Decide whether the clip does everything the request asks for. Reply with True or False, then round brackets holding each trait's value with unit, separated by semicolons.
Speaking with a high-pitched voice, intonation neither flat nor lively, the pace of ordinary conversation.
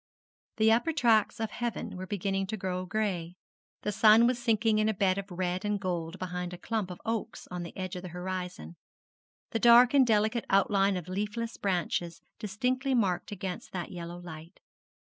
True (195 Hz; 3.6 semitones; 180 wpm)